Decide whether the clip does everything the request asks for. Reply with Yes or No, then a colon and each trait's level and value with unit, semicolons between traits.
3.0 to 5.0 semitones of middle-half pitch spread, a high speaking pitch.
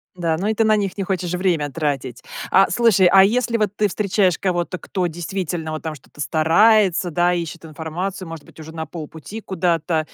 No: average, 3.4 semitones; medium, 175 Hz